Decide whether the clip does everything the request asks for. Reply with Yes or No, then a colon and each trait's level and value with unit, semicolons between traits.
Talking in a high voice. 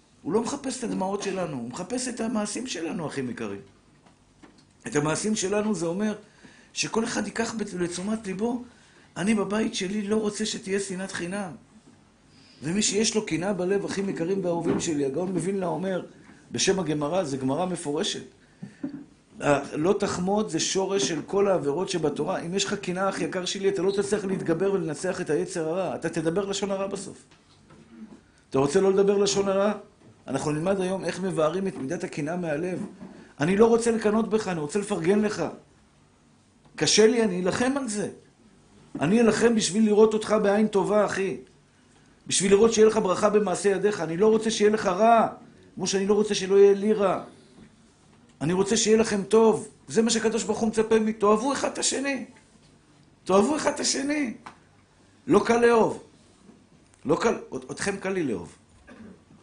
Yes: high, 200 Hz